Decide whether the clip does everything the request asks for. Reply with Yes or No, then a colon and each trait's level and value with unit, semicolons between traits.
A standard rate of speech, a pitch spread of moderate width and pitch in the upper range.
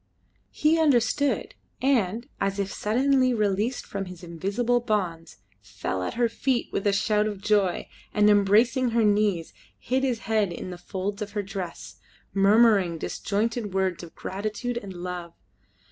Yes: average, 150 wpm; average, 3.7 semitones; high, 205 Hz